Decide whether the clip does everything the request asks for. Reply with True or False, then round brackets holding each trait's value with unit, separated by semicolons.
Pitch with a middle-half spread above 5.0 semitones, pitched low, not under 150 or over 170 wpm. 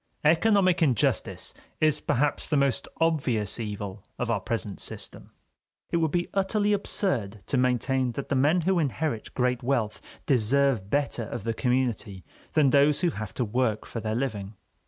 True (5.6 semitones; 130 Hz; 160 wpm)